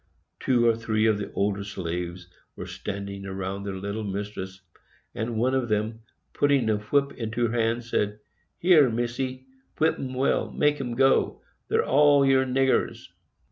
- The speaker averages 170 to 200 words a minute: No, average, 155 wpm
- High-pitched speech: No, low, 115 Hz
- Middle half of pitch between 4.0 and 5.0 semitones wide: Yes, average, 4.5 semitones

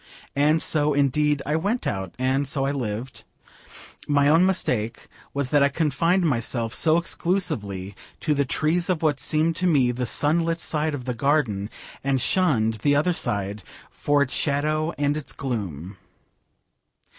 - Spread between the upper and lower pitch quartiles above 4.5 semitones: No, average, 4.2 semitones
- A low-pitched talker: No, medium, 145 Hz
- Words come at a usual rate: Yes, average, 160 wpm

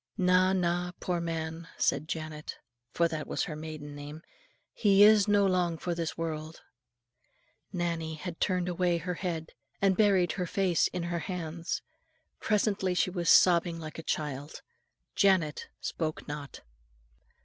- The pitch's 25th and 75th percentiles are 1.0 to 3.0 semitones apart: Yes, narrow, 2.4 semitones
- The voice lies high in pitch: No, medium, 170 Hz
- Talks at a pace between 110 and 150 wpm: Yes, average, 145 wpm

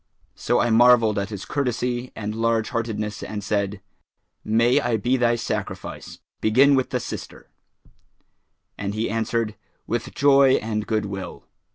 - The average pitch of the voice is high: No, low, 115 Hz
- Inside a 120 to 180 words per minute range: Yes, average, 140 wpm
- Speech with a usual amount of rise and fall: No, narrow, 2.3 semitones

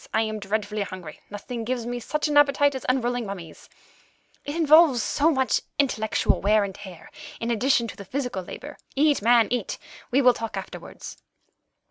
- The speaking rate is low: No, average, 170 wpm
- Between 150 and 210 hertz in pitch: No, high, 240 Hz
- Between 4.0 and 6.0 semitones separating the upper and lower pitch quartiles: Yes, average, 4.8 semitones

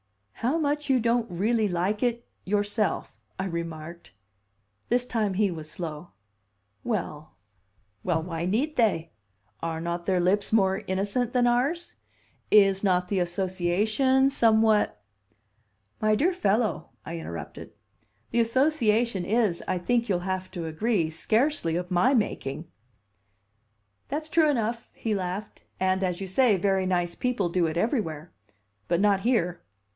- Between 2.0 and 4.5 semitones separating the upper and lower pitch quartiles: No, average, 5.1 semitones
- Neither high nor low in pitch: No, high, 195 Hz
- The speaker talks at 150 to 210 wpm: No, average, 140 wpm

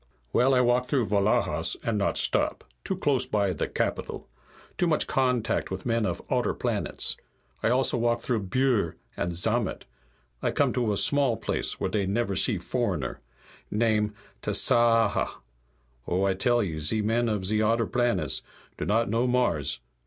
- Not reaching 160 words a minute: No, average, 165 wpm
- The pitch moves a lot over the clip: No, average, 3.5 semitones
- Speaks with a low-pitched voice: Yes, low, 115 Hz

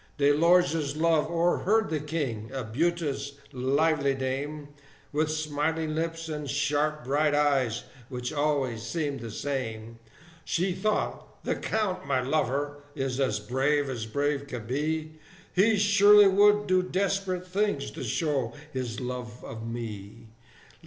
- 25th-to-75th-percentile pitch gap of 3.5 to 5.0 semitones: Yes, average, 4.0 semitones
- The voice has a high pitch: No, medium, 145 Hz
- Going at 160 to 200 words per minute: No, slow, 135 wpm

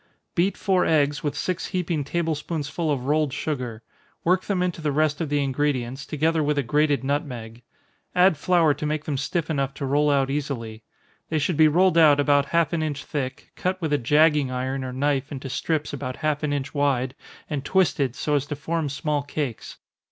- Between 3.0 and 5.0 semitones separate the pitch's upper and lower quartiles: No, narrow, 2.5 semitones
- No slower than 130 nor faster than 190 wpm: No, average, 200 wpm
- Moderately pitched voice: Yes, medium, 145 Hz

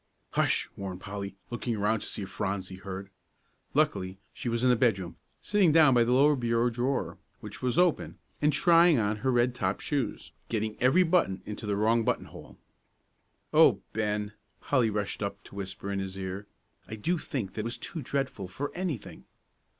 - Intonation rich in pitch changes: No, average, 4.8 semitones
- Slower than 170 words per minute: No, average, 180 wpm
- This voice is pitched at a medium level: No, low, 110 Hz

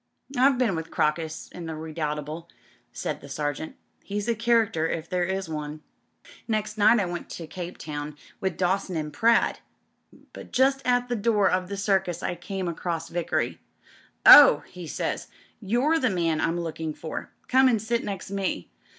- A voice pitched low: No, medium, 180 Hz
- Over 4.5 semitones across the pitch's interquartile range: Yes, average, 5.2 semitones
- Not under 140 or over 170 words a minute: No, average, 180 wpm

